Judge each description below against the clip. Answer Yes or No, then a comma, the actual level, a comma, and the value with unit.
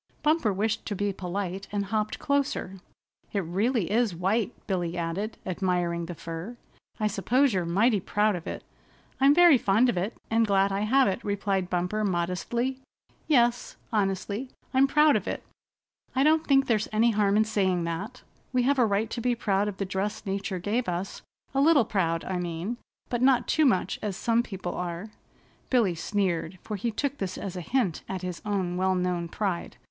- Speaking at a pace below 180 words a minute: No, average, 185 wpm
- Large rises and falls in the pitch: No, average, 4.5 semitones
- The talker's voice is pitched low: No, high, 205 Hz